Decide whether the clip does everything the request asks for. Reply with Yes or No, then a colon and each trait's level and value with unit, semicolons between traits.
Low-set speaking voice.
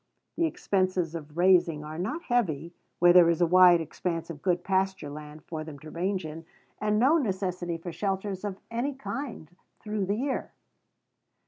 No: medium, 180 Hz